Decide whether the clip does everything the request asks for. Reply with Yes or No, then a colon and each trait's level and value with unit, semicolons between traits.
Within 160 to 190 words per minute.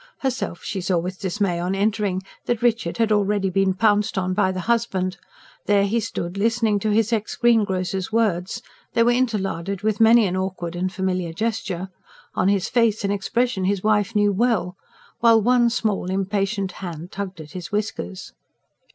Yes: average, 170 wpm